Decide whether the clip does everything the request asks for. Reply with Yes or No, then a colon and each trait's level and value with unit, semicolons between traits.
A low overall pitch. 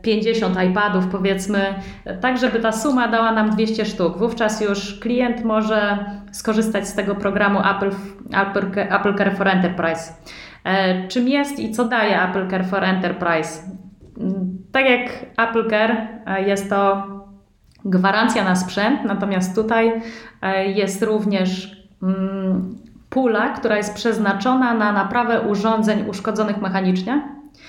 No: high, 205 Hz